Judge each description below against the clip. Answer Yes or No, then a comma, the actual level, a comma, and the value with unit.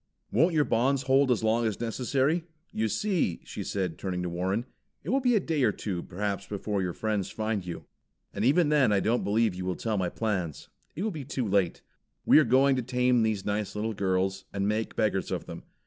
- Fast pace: Yes, fast, 220 wpm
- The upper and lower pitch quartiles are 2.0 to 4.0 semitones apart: No, average, 5.2 semitones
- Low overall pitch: Yes, low, 110 Hz